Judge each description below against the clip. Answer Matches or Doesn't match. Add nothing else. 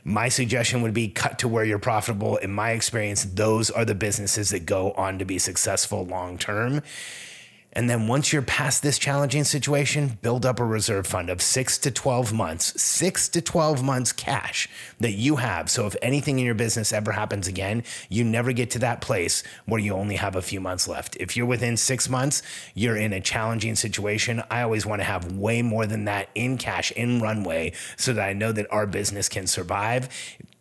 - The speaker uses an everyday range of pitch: Matches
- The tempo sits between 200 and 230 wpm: Matches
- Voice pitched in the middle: Doesn't match